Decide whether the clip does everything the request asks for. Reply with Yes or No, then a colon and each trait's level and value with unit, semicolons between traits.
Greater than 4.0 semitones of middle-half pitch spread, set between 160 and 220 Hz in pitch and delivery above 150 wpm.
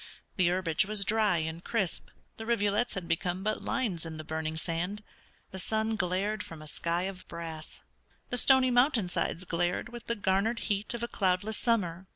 Yes: average, 4.5 semitones; high, 190 Hz; average, 180 wpm